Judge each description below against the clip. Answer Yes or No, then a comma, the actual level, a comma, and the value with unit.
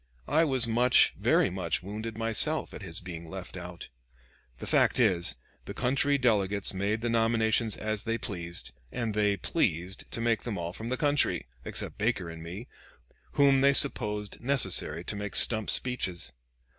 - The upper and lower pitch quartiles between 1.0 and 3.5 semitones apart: No, average, 4.4 semitones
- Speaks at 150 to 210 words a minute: Yes, average, 165 wpm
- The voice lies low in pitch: Yes, low, 110 Hz